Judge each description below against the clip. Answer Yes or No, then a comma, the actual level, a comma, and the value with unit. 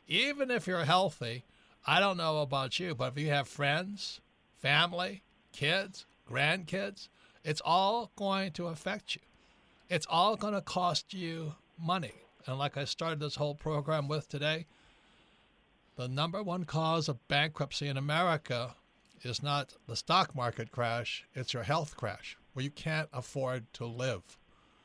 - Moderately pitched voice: Yes, medium, 155 Hz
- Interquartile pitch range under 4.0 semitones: No, average, 4.8 semitones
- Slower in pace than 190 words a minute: Yes, average, 150 wpm